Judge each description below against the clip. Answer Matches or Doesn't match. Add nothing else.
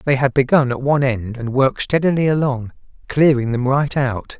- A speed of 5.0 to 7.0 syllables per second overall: Matches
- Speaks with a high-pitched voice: Doesn't match